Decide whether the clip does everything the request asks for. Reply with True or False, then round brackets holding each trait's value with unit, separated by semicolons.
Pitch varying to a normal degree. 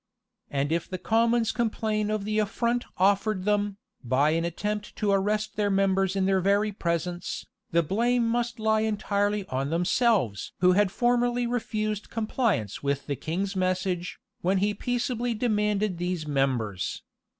True (3.5 semitones)